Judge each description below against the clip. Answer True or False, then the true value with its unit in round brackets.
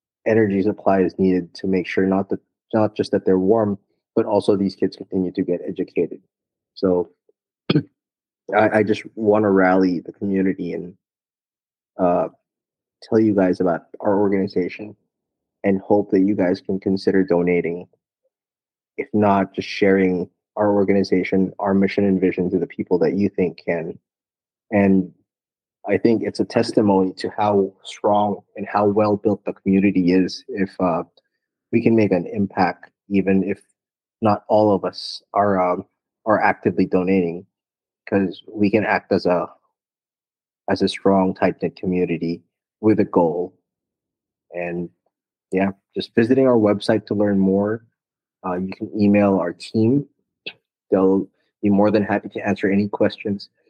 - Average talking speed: True (155 wpm)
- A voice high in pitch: False (100 Hz)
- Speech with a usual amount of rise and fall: False (1.8 semitones)